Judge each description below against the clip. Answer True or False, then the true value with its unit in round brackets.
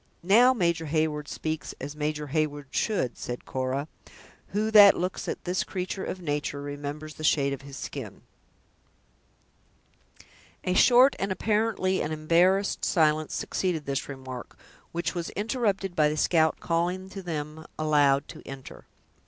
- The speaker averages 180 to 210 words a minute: False (145 wpm)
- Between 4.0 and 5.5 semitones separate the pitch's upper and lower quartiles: True (4.3 semitones)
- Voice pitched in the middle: True (160 Hz)